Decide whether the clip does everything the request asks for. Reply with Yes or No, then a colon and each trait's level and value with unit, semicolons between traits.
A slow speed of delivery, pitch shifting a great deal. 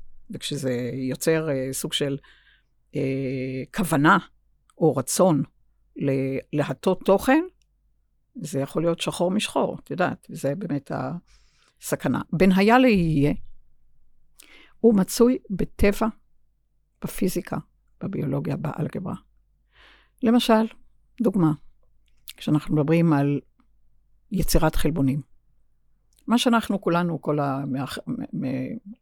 Yes: slow, 90 wpm; wide, 6.9 semitones